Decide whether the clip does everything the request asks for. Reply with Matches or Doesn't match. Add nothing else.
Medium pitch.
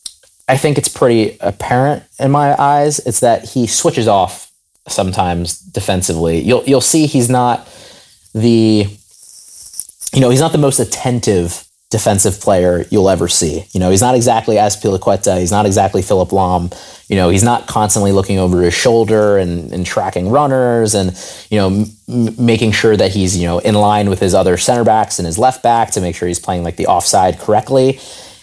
Doesn't match